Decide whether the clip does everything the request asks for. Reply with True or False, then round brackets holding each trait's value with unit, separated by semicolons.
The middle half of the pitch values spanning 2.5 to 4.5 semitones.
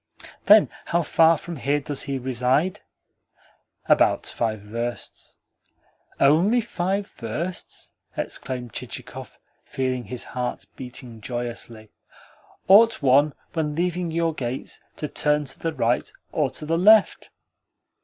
False (5.4 semitones)